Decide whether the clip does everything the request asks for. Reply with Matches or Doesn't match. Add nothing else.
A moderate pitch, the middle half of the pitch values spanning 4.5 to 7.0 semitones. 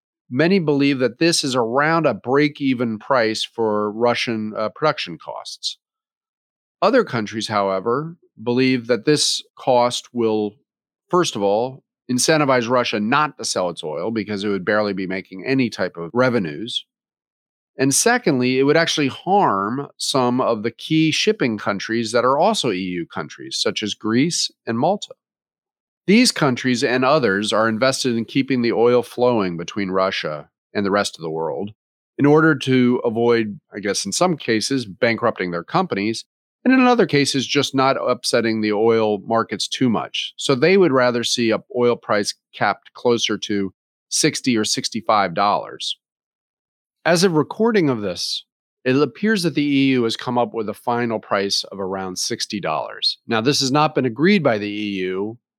Doesn't match